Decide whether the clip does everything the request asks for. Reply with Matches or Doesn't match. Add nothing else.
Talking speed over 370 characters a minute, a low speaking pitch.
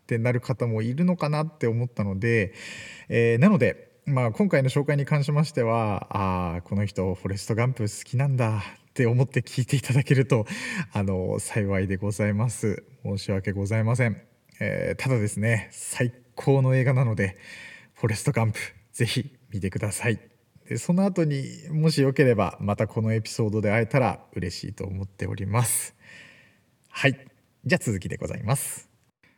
Doesn't match